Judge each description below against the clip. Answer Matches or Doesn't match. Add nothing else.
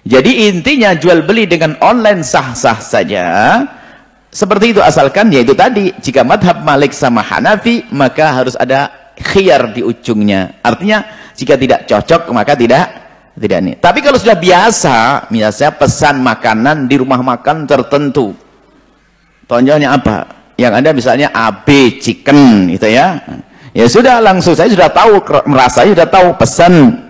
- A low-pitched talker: Doesn't match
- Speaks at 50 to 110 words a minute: Doesn't match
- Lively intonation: Matches